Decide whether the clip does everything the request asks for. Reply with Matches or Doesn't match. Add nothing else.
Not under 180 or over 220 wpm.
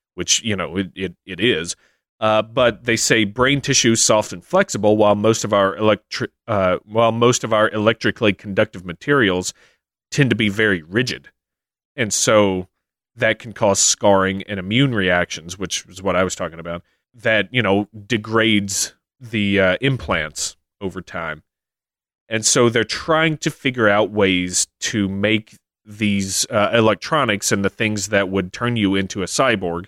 Doesn't match